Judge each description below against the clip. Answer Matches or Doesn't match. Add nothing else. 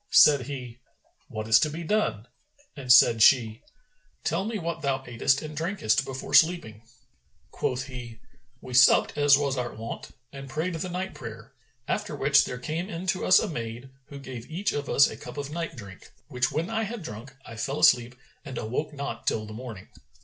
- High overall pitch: Doesn't match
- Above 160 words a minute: Matches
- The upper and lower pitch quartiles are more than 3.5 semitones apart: Matches